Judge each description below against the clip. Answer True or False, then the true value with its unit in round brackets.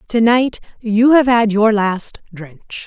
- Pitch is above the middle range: True (220 Hz)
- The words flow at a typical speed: True (170 wpm)